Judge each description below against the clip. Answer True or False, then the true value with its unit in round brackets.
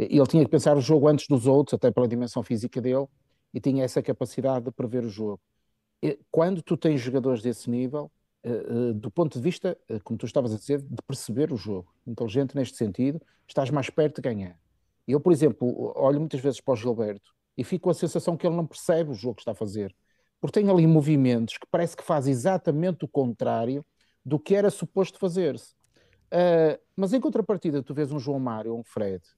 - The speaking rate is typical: False (215 wpm)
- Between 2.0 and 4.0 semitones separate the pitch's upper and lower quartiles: False (4.7 semitones)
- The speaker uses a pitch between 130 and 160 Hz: True (140 Hz)